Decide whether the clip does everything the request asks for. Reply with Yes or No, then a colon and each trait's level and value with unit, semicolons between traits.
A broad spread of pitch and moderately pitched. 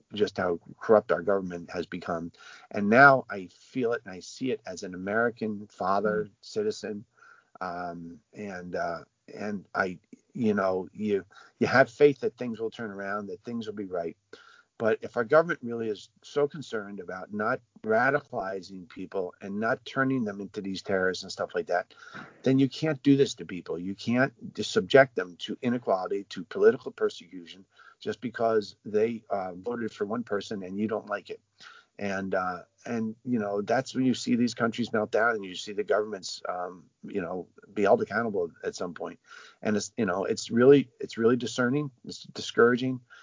No: wide, 6.0 semitones; low, 115 Hz